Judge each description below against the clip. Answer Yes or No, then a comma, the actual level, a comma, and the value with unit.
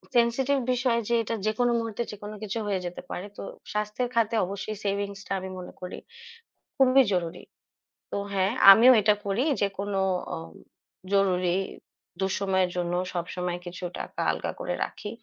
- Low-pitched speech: No, high, 200 Hz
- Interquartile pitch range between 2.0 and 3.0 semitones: No, average, 3.6 semitones